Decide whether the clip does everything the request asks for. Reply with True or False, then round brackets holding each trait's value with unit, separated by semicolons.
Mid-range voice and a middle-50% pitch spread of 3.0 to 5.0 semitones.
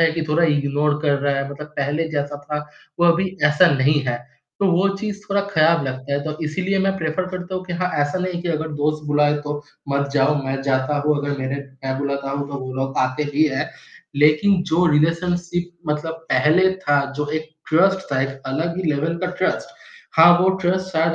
True (150 Hz; 3.7 semitones)